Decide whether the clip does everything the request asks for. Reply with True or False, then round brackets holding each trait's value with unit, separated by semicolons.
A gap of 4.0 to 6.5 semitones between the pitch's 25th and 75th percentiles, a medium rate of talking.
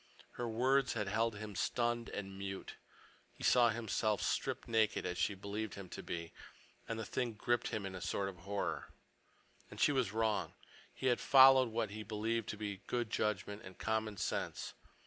False (2.7 semitones; 185 wpm)